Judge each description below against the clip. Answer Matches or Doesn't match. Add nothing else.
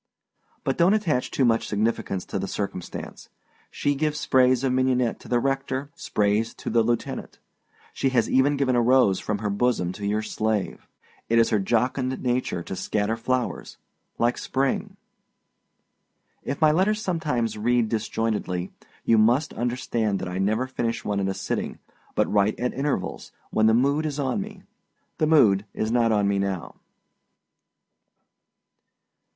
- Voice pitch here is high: Doesn't match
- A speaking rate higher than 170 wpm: Doesn't match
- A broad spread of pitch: Doesn't match